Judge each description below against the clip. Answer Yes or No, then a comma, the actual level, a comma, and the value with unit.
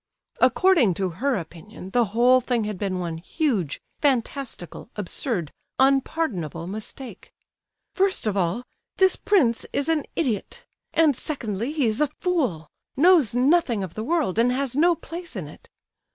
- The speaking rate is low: No, average, 145 wpm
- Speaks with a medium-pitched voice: No, high, 245 Hz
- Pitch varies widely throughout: Yes, wide, 7.6 semitones